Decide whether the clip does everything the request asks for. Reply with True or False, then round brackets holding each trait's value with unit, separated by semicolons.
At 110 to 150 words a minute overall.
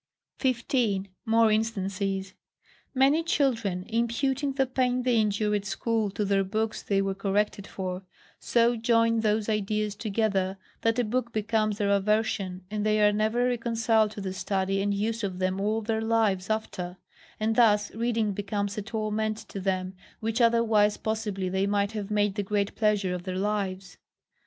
False (165 wpm)